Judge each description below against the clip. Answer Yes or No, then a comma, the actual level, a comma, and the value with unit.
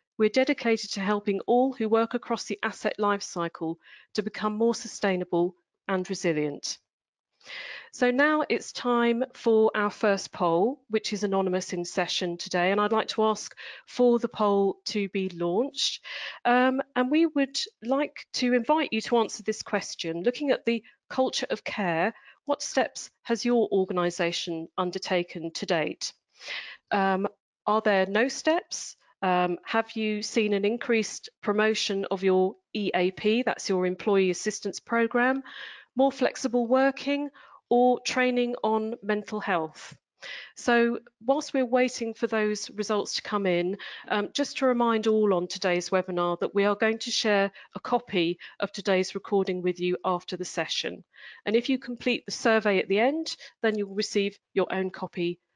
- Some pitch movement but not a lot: Yes, average, 4.3 semitones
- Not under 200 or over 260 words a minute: No, average, 155 wpm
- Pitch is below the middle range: No, high, 215 Hz